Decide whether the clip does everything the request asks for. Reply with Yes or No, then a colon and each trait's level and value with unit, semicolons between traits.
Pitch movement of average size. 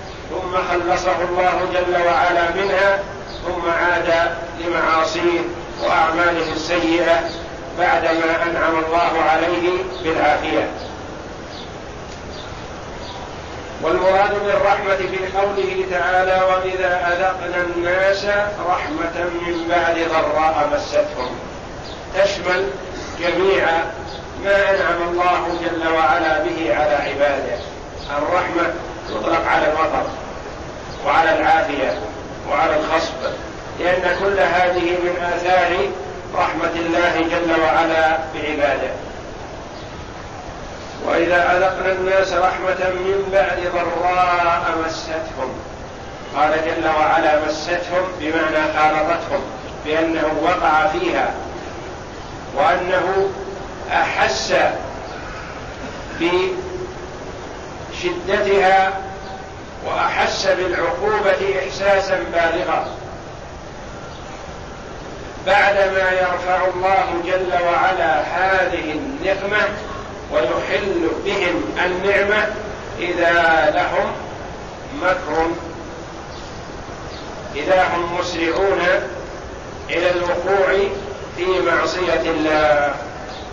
No: narrow, 2.3 semitones